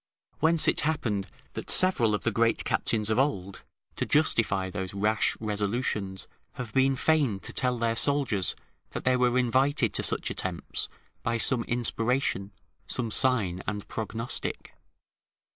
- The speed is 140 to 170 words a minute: Yes, average, 145 wpm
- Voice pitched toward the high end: No, low, 115 Hz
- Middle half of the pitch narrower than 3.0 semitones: No, average, 3.9 semitones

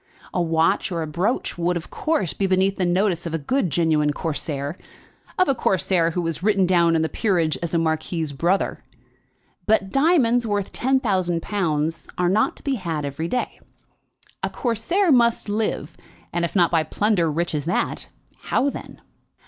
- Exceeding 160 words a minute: Yes, average, 180 wpm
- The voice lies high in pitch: No, medium, 175 Hz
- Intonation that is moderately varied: Yes, average, 4.5 semitones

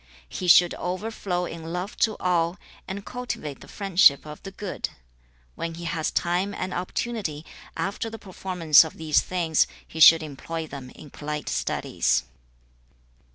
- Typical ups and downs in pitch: Yes, average, 3.2 semitones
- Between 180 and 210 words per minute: No, average, 150 wpm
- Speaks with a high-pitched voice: No, medium, 175 Hz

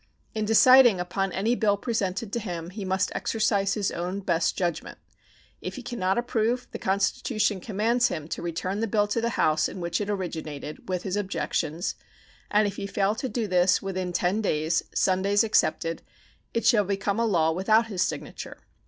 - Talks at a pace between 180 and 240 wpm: Yes, average, 185 wpm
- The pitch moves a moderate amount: Yes, average, 3.5 semitones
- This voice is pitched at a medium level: No, high, 195 Hz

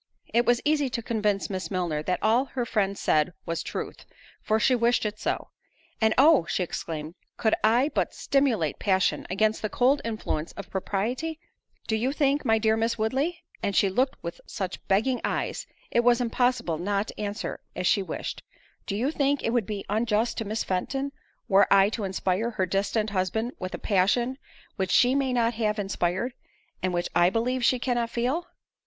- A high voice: Yes, high, 220 Hz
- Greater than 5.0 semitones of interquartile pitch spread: No, average, 4.1 semitones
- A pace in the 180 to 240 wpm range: Yes, average, 185 wpm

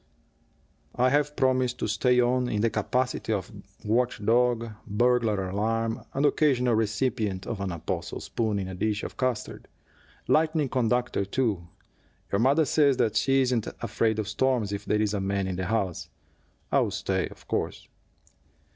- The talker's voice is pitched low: Yes, low, 115 Hz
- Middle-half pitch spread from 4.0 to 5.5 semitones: No, average, 3.6 semitones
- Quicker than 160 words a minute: No, average, 155 wpm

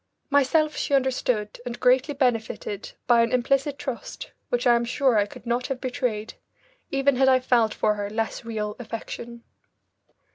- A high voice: Yes, high, 245 Hz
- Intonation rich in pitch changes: No, average, 2.7 semitones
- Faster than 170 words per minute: No, average, 160 wpm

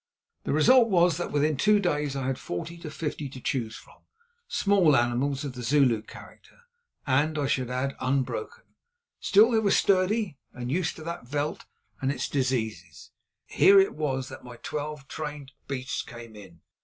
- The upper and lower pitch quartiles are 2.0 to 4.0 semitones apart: No, average, 4.8 semitones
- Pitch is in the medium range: Yes, medium, 145 Hz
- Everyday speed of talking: Yes, average, 170 wpm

